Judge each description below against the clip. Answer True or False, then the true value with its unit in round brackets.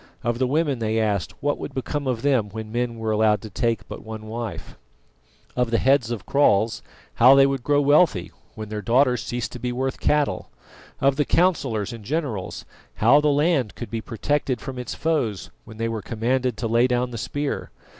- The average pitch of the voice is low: True (120 Hz)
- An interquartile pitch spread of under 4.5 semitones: True (3.8 semitones)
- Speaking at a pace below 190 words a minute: False (200 wpm)